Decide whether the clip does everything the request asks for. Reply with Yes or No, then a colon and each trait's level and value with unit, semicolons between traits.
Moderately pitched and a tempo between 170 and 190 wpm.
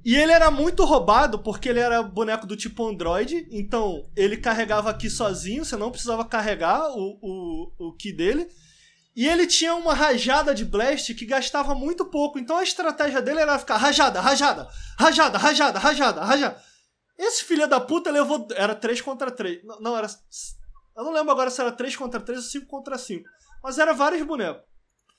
No: very high, 265 Hz; fast, 185 wpm